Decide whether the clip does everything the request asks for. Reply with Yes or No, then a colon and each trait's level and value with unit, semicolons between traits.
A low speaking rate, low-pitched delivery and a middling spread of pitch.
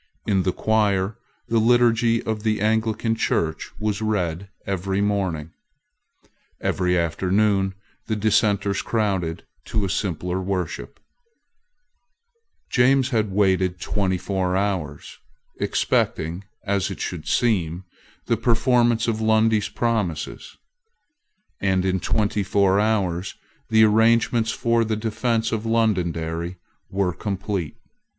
Yes: slow, 110 wpm; low, 100 Hz; average, 3.1 semitones